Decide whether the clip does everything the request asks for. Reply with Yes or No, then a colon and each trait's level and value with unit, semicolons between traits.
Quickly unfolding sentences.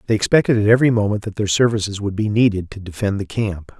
Yes: fast, 235 wpm